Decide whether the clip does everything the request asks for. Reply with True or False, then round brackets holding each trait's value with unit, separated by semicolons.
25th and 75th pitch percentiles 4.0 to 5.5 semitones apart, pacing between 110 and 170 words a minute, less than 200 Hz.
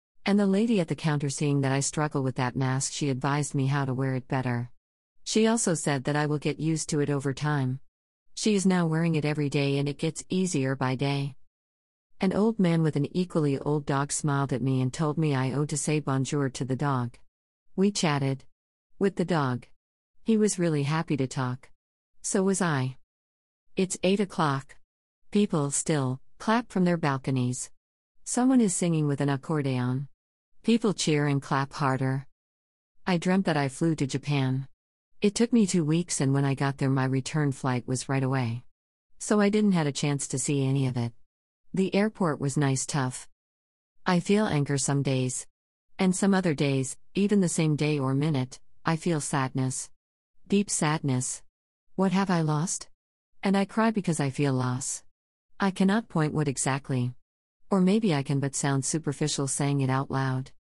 False (4.3 semitones; 185 wpm; 140 Hz)